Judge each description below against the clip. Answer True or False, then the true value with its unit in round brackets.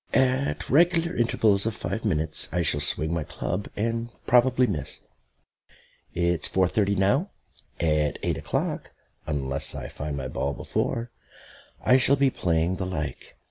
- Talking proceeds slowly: False (145 wpm)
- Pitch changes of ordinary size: False (7.7 semitones)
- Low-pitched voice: True (95 Hz)